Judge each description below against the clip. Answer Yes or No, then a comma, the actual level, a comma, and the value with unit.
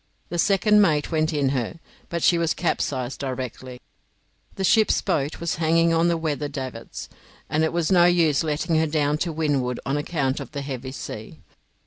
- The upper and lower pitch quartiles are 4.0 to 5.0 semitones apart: No, average, 3.5 semitones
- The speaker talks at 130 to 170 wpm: No, average, 180 wpm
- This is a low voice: No, medium, 155 Hz